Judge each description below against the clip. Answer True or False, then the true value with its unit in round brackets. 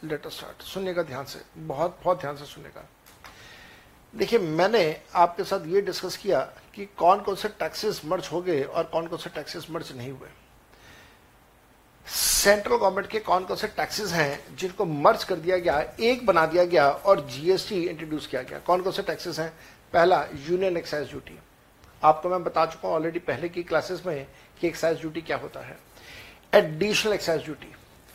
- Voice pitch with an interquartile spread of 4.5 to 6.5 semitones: False (3.4 semitones)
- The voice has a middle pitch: True (170 Hz)